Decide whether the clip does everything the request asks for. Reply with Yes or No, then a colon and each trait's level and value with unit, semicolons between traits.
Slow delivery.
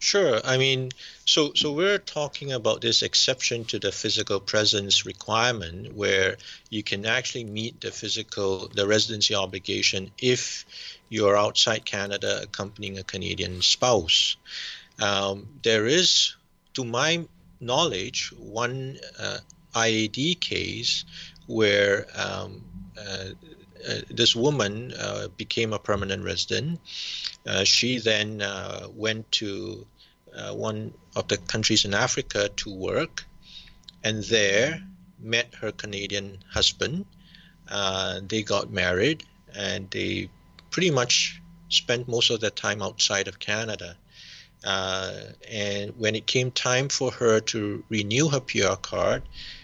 Yes: slow, 125 wpm